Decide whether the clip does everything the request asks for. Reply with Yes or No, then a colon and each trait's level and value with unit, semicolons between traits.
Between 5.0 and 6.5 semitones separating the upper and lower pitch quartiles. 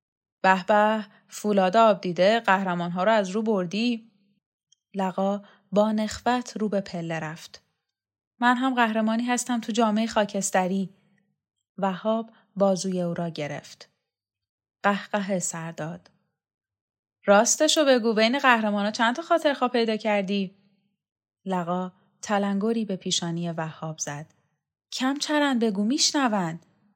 No: average, 4.6 semitones